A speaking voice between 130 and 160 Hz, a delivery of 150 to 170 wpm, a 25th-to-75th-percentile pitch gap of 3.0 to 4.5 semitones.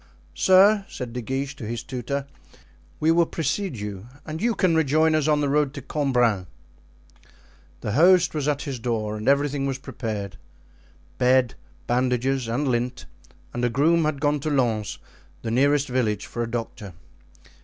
Yes: low, 135 Hz; average, 160 wpm; average, 4.1 semitones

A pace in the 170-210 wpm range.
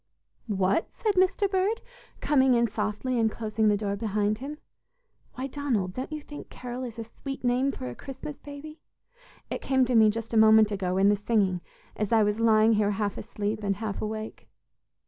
Yes: average, 190 wpm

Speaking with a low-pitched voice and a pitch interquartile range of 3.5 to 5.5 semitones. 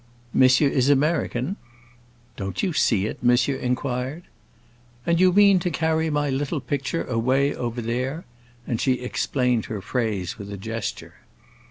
Yes: low, 130 Hz; average, 4.0 semitones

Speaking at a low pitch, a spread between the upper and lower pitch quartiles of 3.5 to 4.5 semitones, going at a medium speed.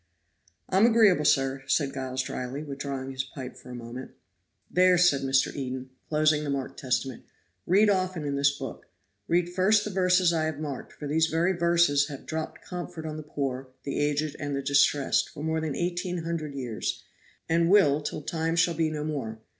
No: medium, 150 Hz; average, 3.8 semitones; average, 185 wpm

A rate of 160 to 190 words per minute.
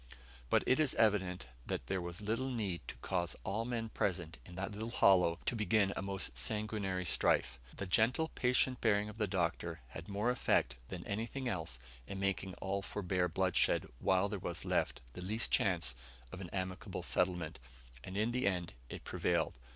Yes: average, 180 wpm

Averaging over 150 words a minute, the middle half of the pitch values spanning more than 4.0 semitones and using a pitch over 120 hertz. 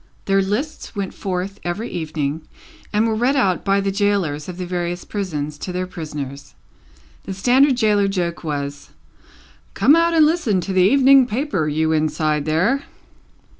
Yes: average, 160 wpm; wide, 5.6 semitones; high, 190 Hz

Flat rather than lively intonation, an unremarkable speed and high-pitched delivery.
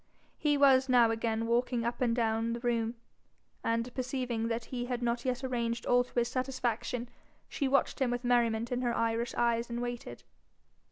Yes: narrow, 1.4 semitones; average, 180 wpm; high, 240 Hz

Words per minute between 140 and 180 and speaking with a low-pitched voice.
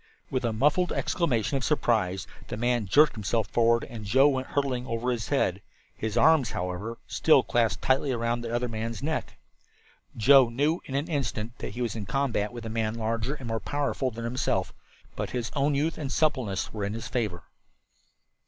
No: average, 190 wpm; low, 120 Hz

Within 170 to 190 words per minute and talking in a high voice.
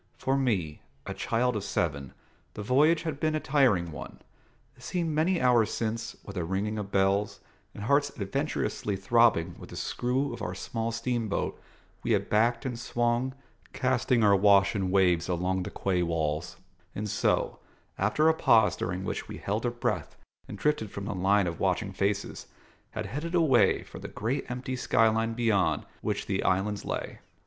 No: average, 175 wpm; low, 110 Hz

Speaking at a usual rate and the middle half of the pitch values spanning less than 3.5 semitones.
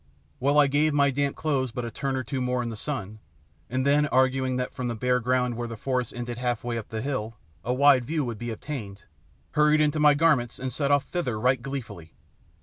No: fast, 230 wpm; average, 3.1 semitones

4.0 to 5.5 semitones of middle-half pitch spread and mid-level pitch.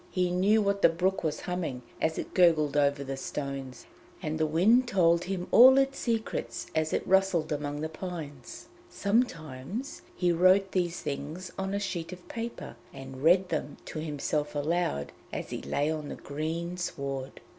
Yes: average, 4.4 semitones; medium, 165 Hz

